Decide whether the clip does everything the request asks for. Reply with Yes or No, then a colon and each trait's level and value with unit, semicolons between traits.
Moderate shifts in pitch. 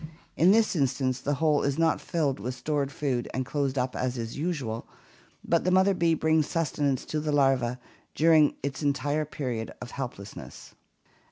Yes: average, 3.6 semitones